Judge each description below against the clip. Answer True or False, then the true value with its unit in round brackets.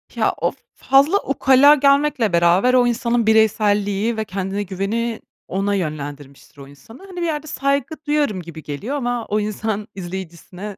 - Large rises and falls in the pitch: True (6.0 semitones)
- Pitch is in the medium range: False (215 Hz)